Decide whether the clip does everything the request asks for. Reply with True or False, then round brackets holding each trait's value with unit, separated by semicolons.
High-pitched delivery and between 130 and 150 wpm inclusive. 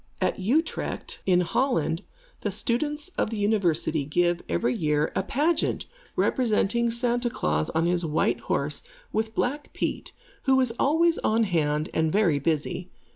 True (200 Hz; 145 wpm)